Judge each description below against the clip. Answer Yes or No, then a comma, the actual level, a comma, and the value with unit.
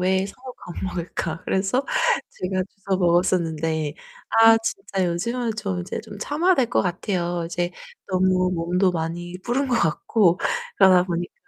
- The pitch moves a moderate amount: Yes, average, 3.0 semitones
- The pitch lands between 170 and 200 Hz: Yes, medium, 185 Hz